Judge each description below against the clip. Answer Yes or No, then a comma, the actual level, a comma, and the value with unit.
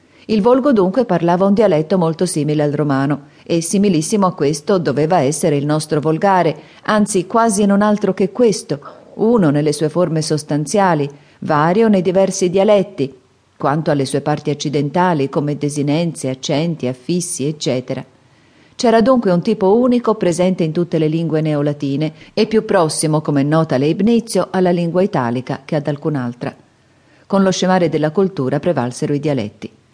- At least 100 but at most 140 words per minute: No, average, 150 wpm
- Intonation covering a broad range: No, average, 4.9 semitones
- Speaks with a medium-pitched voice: Yes, medium, 160 Hz